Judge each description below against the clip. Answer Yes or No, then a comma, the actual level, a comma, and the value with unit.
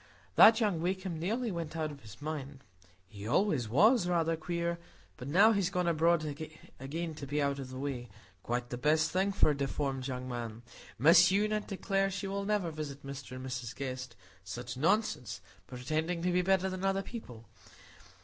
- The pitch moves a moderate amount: No, wide, 6.4 semitones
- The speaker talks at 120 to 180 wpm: Yes, average, 175 wpm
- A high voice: No, medium, 155 Hz